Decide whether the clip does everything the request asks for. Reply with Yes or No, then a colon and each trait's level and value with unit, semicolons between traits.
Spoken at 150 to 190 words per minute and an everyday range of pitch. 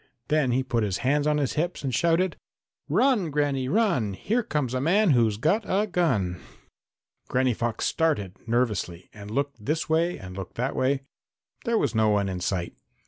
No: average, 180 wpm; wide, 7.1 semitones